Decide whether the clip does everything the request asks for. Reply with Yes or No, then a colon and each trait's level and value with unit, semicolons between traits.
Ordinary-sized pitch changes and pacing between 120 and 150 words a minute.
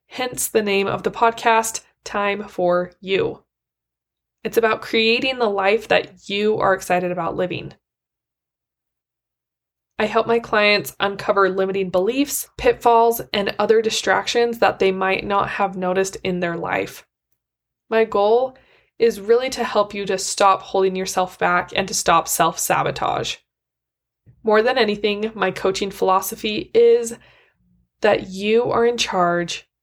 Yes: average, 3.2 semitones; average, 140 wpm